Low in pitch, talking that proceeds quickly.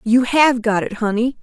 No: high, 235 Hz; fast, 210 wpm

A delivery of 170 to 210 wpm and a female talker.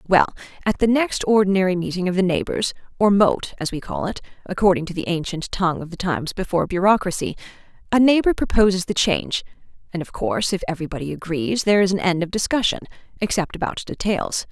Yes: average, 185 wpm; female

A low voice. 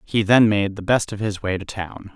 Yes: low, 100 Hz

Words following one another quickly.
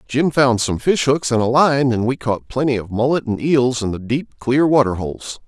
Yes: fast, 230 wpm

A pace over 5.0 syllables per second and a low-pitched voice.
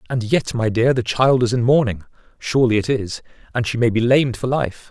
Yes: 5.7 syllables/s; low, 120 Hz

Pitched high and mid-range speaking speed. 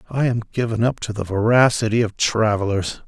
No: low, 110 Hz; average, 175 wpm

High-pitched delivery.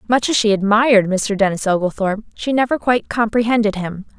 Yes: high, 215 Hz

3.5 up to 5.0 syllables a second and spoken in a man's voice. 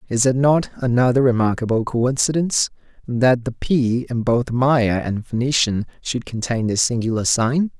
Yes: 4.6 syllables/s; male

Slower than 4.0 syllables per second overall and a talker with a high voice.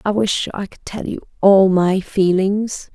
Yes: 3.8 syllables/s; high, 195 Hz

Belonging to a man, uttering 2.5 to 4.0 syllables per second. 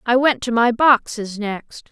No: female; 3.9 syllables/s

